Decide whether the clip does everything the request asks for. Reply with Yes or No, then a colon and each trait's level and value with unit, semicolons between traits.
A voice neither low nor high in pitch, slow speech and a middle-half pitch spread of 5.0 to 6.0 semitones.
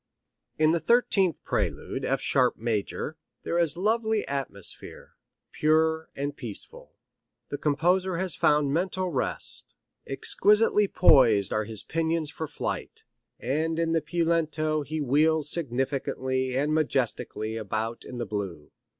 No: medium, 150 Hz; slow, 130 wpm; average, 4.5 semitones